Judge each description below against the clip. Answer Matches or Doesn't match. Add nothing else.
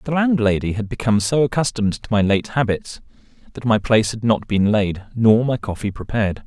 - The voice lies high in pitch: Doesn't match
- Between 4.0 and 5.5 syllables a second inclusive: Doesn't match